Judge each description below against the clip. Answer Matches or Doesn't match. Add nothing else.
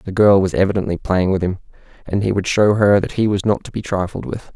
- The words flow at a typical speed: Doesn't match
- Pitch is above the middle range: Doesn't match